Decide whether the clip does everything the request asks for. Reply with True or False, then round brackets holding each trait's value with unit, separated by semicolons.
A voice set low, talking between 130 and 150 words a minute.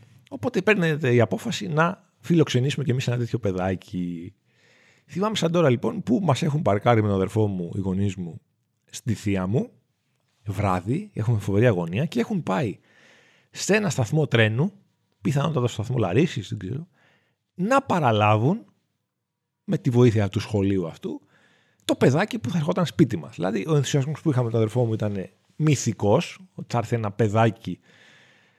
False (125 Hz; 160 wpm)